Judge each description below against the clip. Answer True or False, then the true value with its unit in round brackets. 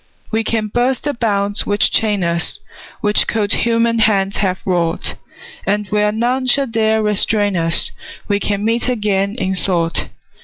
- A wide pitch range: False (2.5 semitones)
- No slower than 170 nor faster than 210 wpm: False (155 wpm)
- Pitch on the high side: True (210 Hz)